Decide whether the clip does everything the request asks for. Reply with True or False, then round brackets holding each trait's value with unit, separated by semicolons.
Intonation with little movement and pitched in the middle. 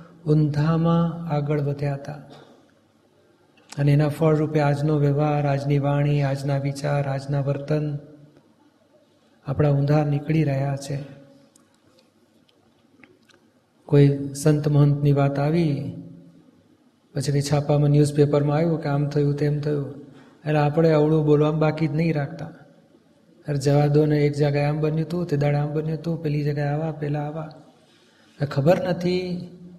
True (1.4 semitones; 150 Hz)